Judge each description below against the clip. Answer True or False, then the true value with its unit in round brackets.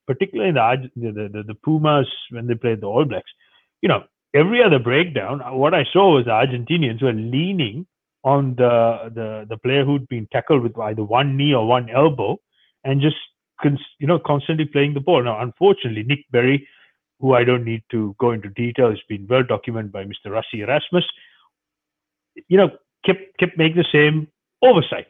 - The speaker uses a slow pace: False (185 wpm)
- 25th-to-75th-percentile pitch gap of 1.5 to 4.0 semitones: False (4.7 semitones)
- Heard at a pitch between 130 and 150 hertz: True (135 Hz)